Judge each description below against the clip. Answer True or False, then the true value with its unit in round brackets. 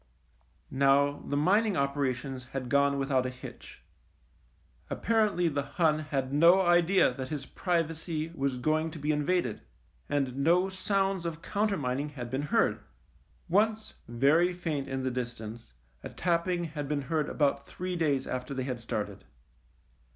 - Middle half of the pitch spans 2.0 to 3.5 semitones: False (4.5 semitones)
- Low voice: False (145 Hz)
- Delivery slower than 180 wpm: True (150 wpm)